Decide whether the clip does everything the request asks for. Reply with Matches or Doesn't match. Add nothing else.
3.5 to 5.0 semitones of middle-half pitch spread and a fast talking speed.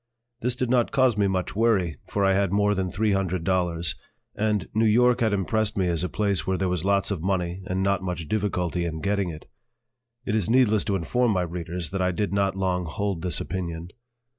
Doesn't match